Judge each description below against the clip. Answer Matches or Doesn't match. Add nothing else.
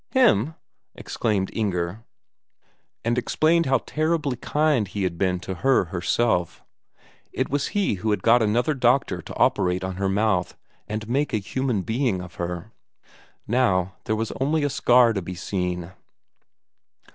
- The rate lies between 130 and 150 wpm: Matches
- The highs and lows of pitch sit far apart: Matches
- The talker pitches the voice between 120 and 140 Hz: Doesn't match